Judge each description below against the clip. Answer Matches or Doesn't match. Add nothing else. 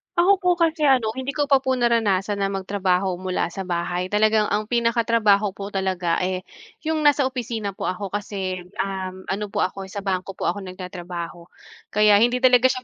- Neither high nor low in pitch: Doesn't match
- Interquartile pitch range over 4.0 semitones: Matches